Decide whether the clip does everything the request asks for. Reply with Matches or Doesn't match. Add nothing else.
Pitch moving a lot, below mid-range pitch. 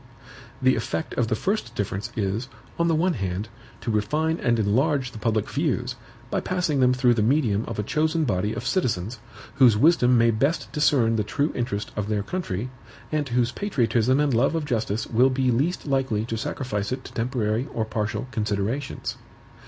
Doesn't match